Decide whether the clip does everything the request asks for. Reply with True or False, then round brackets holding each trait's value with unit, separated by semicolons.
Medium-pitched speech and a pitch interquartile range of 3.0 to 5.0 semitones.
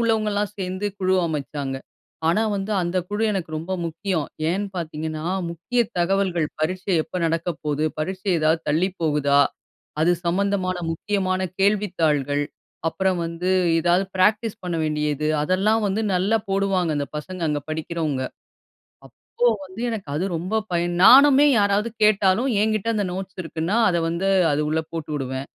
True (180 Hz; 4.0 semitones)